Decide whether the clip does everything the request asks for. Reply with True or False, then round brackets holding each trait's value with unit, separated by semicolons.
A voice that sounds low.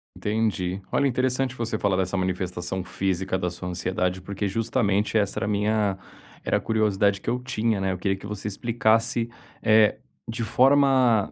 True (105 Hz)